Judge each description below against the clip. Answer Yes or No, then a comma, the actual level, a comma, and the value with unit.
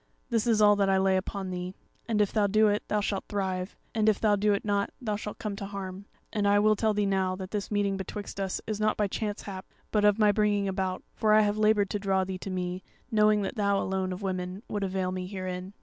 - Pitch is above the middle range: Yes, high, 200 Hz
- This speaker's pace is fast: Yes, fast, 255 wpm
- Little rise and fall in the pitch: Yes, narrow, 1.8 semitones